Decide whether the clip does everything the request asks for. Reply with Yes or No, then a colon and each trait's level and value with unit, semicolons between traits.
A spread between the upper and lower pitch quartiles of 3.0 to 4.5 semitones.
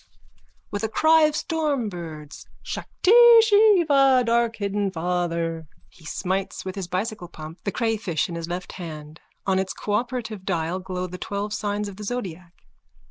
No: average, 5.0 semitones